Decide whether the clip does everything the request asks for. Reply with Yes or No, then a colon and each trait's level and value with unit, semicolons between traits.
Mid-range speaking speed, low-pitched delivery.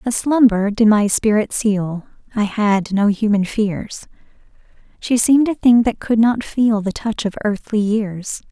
No: average, 170 wpm; high, 215 Hz